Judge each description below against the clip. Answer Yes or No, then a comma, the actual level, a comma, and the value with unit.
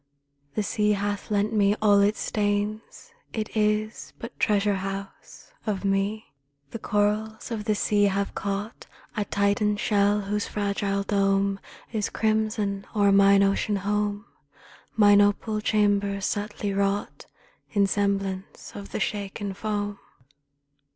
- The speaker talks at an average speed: No, slow, 130 wpm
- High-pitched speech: Yes, high, 205 Hz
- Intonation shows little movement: Yes, narrow, 1.1 semitones